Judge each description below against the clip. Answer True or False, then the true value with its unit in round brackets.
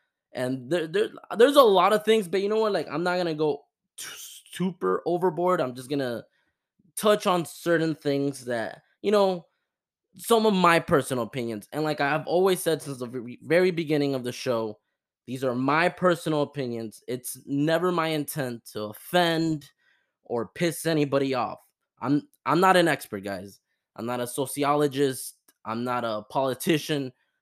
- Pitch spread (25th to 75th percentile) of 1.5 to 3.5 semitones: False (5.6 semitones)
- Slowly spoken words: False (175 wpm)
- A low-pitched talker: False (145 Hz)